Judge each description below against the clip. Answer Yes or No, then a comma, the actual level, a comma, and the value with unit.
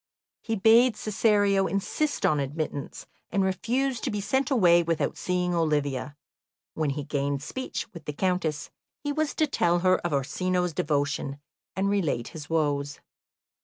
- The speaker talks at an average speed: Yes, average, 150 wpm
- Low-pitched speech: No, medium, 175 Hz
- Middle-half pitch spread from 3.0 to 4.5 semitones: No, wide, 5.6 semitones